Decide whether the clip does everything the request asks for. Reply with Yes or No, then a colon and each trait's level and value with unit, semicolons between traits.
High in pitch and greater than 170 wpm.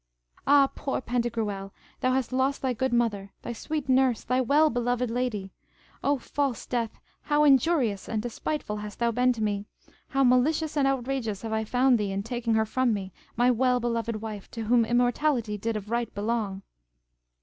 Yes: high, 240 Hz; average, 180 wpm